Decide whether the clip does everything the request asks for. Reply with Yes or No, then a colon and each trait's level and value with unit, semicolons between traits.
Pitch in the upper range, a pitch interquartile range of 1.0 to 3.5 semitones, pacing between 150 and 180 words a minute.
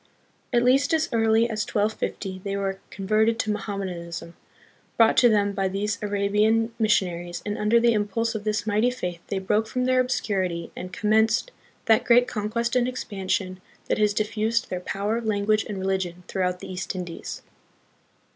Yes: high, 210 Hz; average, 2.8 semitones; average, 165 wpm